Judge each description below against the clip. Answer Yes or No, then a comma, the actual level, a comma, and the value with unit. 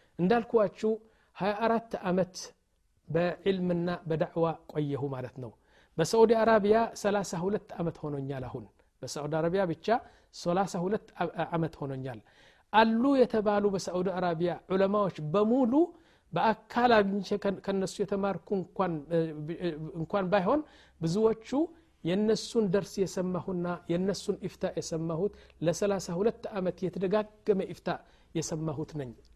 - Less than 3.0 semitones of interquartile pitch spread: No, average, 4.3 semitones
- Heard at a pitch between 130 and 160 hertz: No, high, 190 Hz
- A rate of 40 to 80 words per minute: No, average, 90 wpm